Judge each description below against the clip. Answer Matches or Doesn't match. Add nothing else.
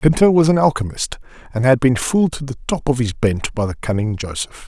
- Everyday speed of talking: Doesn't match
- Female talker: Doesn't match